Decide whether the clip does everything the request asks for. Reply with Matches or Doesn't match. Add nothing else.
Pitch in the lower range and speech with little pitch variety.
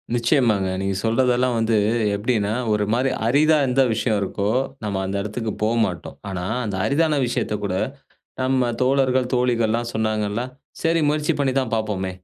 Doesn't match